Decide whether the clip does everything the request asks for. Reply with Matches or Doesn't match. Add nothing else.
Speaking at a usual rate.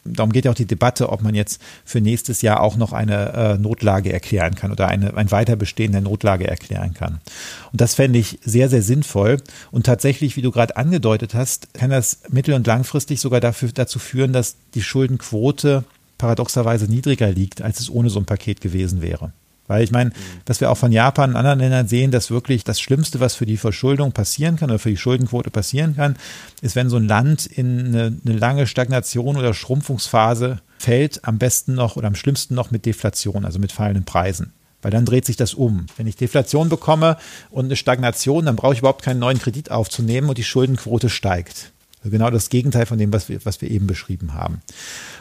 Doesn't match